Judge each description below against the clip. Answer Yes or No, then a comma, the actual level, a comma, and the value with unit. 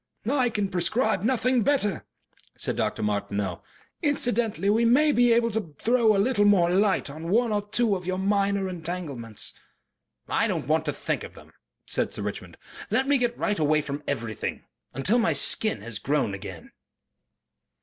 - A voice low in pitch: No, high, 200 Hz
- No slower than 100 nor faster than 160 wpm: No, average, 170 wpm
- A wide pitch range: Yes, wide, 7.5 semitones